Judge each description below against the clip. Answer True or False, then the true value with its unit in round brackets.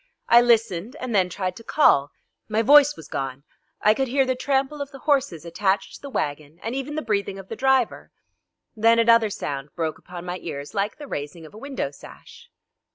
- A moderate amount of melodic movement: False (7.2 semitones)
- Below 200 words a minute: False (205 wpm)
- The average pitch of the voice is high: True (220 Hz)